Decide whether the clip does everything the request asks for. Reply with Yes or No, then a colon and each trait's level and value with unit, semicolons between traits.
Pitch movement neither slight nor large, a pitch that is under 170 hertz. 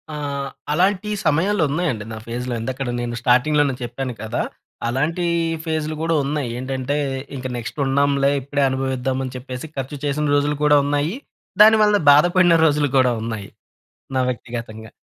Yes: average, 3.3 semitones; medium, 140 Hz